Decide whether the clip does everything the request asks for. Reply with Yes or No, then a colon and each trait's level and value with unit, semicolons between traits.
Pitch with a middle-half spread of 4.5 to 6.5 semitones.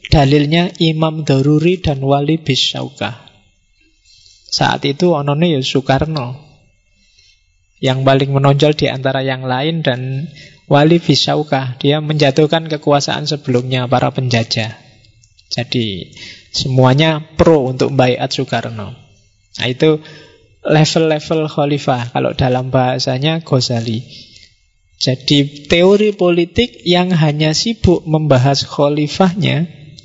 No: average, 3.9 semitones